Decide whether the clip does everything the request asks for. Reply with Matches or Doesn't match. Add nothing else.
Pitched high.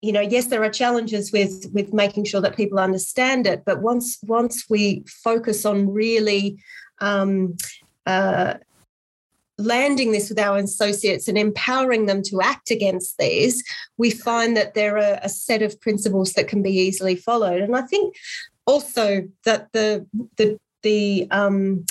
Matches